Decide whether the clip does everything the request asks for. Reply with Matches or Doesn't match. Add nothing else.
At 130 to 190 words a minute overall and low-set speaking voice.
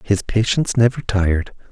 Matches